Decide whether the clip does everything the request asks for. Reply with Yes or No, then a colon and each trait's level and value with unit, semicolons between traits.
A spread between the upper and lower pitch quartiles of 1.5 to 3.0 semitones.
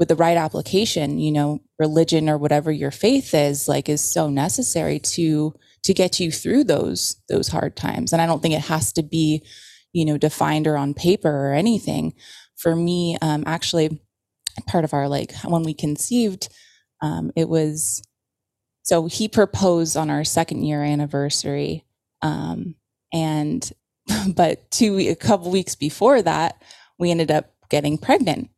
Yes: narrow, 2.6 semitones